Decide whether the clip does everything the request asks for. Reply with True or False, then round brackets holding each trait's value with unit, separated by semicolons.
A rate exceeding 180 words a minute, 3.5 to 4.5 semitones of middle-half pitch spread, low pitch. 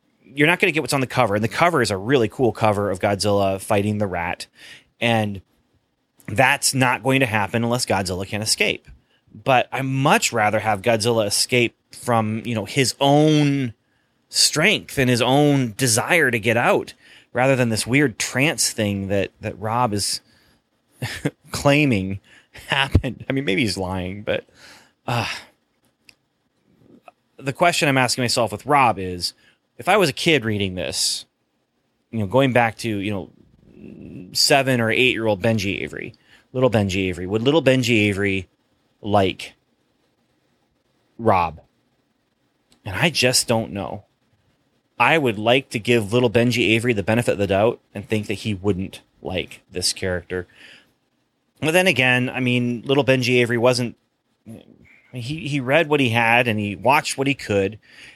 False (160 wpm; 4.2 semitones; 115 Hz)